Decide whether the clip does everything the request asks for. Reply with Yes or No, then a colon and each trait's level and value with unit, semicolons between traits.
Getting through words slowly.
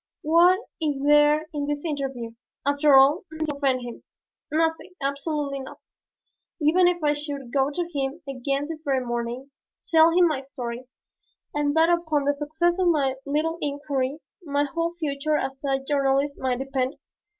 No: average, 160 wpm